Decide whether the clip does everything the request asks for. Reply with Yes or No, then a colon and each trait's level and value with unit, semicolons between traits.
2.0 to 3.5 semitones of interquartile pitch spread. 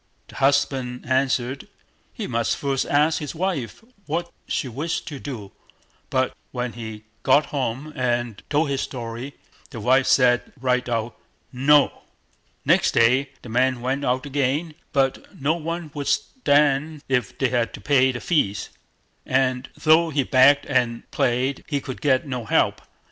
Yes: average, 2.7 semitones